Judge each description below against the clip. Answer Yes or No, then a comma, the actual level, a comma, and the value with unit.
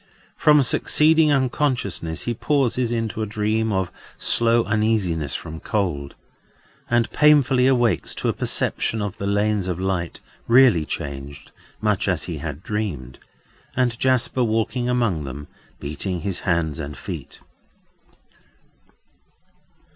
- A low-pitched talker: Yes, low, 105 Hz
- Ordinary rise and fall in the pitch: No, wide, 6.5 semitones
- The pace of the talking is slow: Yes, slow, 115 wpm